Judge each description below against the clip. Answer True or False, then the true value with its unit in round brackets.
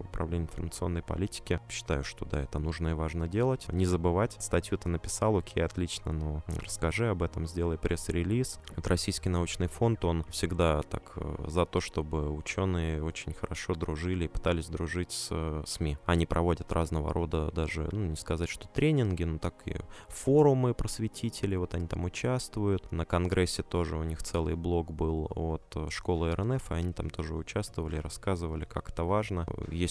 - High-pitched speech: False (85 Hz)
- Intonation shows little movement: False (3.3 semitones)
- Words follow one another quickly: True (170 wpm)